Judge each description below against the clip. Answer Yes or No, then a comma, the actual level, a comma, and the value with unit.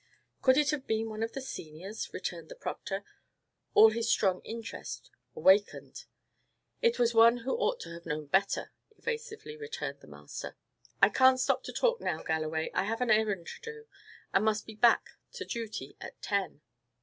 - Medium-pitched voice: No, high, 225 Hz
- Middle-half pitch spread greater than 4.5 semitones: Yes, average, 5.3 semitones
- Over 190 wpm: No, average, 175 wpm